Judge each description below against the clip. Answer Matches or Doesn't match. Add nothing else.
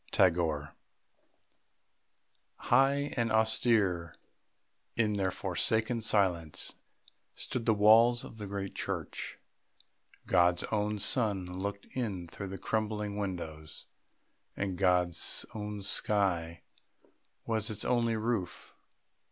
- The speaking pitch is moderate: Doesn't match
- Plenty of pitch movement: Doesn't match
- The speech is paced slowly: Matches